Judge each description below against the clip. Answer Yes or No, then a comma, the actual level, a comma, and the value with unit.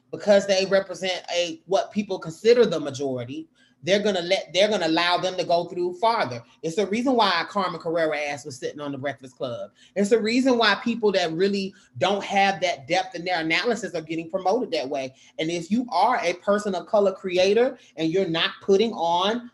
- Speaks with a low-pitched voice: No, medium, 185 Hz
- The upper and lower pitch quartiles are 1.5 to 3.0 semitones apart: No, average, 4.1 semitones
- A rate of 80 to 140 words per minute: No, fast, 205 wpm